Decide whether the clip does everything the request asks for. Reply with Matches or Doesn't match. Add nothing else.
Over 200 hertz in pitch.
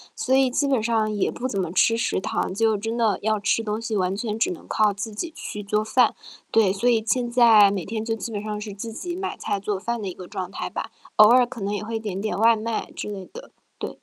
Matches